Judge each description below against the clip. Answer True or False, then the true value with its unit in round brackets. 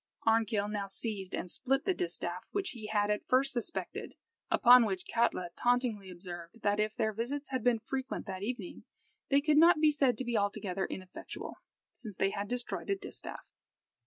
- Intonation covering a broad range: False (4.4 semitones)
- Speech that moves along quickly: False (180 wpm)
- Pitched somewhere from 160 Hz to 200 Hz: False (220 Hz)